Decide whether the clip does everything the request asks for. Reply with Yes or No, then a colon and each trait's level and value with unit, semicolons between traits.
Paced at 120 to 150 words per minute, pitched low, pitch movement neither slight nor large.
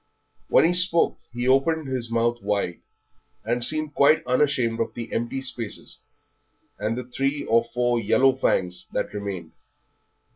Yes: average, 145 wpm; low, 120 Hz; average, 3.0 semitones